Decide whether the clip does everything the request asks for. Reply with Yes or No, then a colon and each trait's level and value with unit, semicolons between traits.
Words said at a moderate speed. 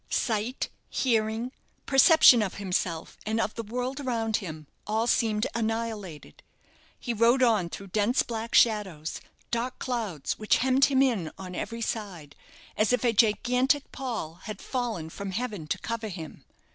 Yes: average, 150 wpm